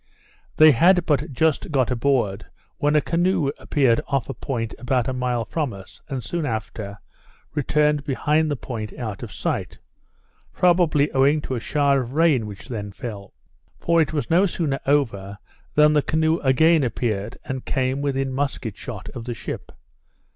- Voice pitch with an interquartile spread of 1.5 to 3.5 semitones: No, average, 4.4 semitones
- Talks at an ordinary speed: Yes, average, 170 wpm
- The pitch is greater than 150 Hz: No, low, 135 Hz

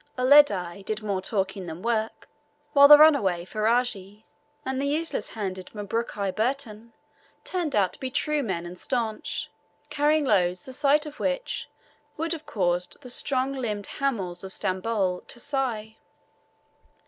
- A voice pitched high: Yes, high, 225 Hz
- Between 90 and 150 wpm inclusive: Yes, average, 145 wpm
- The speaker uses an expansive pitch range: Yes, wide, 6.3 semitones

